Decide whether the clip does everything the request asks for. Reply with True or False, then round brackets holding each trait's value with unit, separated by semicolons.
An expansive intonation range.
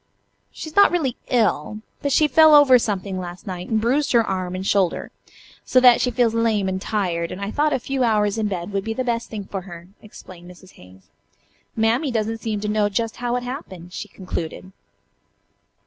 False (4.7 semitones)